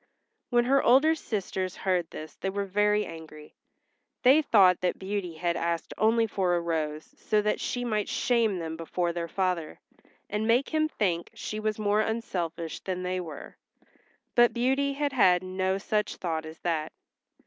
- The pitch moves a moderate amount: Yes, average, 4.6 semitones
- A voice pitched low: No, high, 190 Hz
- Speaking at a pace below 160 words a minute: No, average, 170 wpm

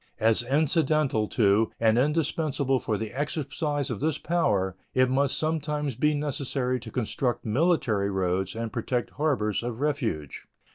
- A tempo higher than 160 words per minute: No, average, 140 wpm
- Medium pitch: No, low, 130 Hz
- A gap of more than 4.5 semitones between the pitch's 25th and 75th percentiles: Yes, average, 5.1 semitones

